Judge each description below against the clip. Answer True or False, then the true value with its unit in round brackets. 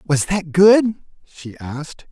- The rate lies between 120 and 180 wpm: True (140 wpm)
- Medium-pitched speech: True (170 Hz)